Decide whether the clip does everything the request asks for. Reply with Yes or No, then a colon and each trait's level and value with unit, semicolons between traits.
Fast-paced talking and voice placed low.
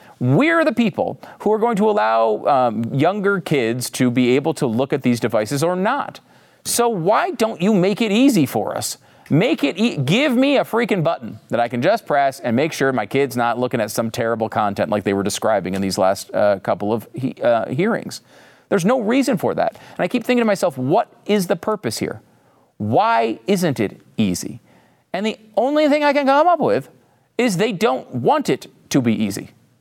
No: fast, 210 wpm; medium, 180 Hz